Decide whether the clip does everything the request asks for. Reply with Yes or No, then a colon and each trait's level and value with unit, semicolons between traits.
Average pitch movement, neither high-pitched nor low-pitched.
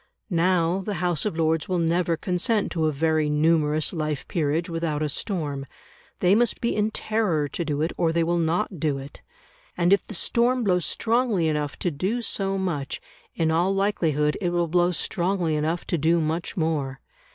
Yes: average, 3.3 semitones; medium, 170 Hz